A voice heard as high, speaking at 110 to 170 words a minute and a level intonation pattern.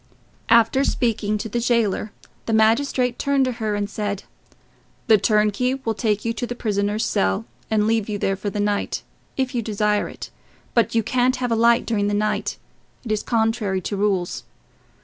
No: high, 220 Hz; average, 180 wpm; narrow, 2.3 semitones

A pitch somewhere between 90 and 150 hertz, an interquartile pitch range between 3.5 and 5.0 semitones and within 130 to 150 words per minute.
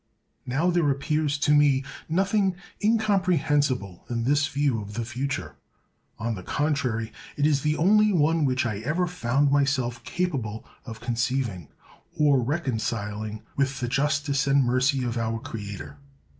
Yes: low, 135 Hz; average, 4.4 semitones; average, 145 wpm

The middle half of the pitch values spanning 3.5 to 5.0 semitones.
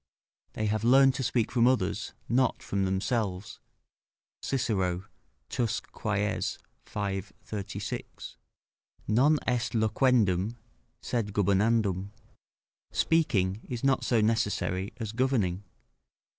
Yes: average, 3.8 semitones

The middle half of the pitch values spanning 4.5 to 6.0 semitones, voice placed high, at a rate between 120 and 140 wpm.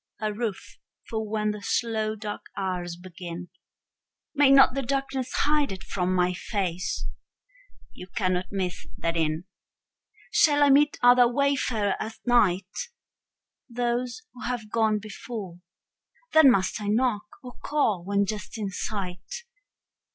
Yes: average, 4.9 semitones; high, 215 Hz; slow, 135 wpm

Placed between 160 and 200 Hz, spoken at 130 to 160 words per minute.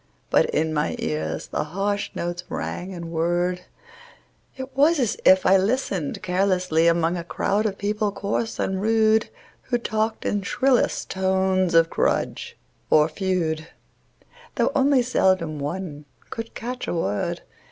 Yes: high, 190 Hz; average, 140 wpm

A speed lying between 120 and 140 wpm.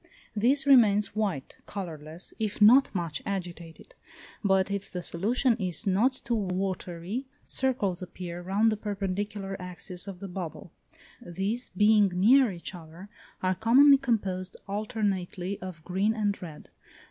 Yes: slow, 135 wpm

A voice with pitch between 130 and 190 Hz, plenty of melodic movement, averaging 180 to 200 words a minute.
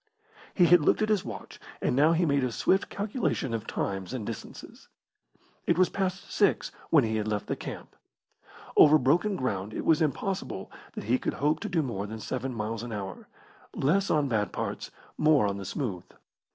Yes: low, 135 Hz; wide, 7.9 semitones; average, 190 wpm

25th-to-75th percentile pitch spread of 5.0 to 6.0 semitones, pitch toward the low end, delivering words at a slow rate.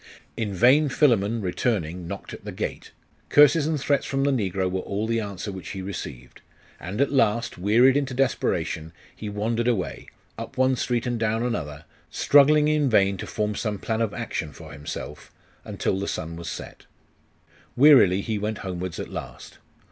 No: wide, 5.4 semitones; low, 110 Hz; average, 175 wpm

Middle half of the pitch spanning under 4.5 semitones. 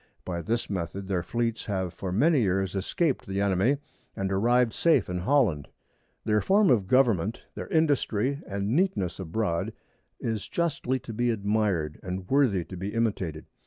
No: average, 5.0 semitones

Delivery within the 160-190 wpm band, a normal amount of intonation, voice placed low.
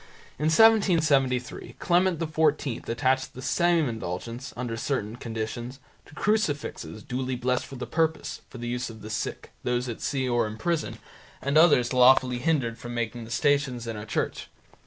Yes: average, 165 wpm; average, 4.3 semitones; low, 125 Hz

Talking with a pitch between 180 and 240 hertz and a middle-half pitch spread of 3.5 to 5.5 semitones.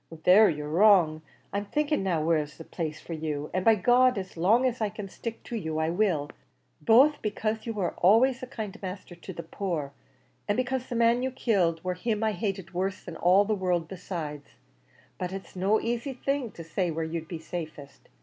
Yes: high, 190 Hz; average, 5.2 semitones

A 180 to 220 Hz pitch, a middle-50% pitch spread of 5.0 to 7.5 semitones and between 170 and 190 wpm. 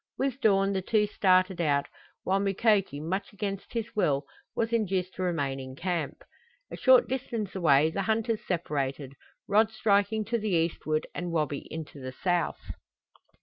No: high, 190 Hz; wide, 5.4 semitones; average, 155 wpm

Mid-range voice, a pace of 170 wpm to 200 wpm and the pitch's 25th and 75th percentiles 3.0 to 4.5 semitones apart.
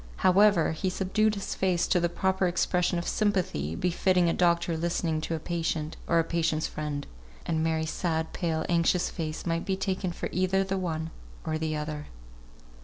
No: medium, 170 Hz; average, 180 wpm; narrow, 2.6 semitones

